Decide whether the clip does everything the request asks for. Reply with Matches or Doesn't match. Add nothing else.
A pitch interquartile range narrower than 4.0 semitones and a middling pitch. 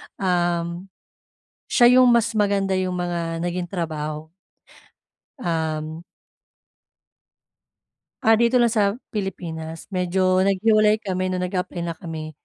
Matches